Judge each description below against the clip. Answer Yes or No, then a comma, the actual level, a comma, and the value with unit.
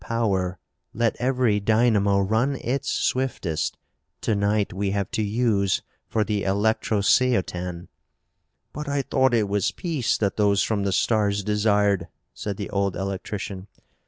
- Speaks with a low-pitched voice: Yes, low, 105 Hz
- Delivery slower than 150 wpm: Yes, slow, 135 wpm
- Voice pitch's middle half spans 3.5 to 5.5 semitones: No, average, 2.7 semitones